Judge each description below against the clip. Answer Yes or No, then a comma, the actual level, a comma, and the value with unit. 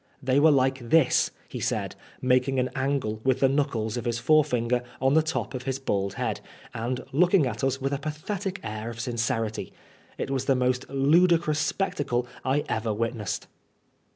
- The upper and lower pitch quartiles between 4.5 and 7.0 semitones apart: No, average, 3.6 semitones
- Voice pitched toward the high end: No, low, 130 Hz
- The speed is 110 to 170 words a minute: No, average, 180 wpm